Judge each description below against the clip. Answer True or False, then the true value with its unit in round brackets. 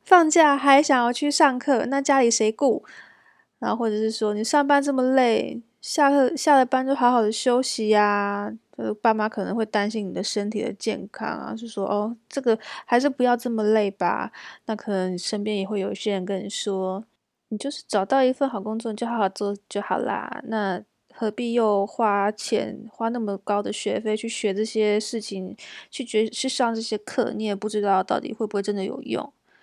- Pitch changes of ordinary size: True (3.5 semitones)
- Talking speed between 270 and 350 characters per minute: True (285 characters per minute)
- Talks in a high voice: True (220 Hz)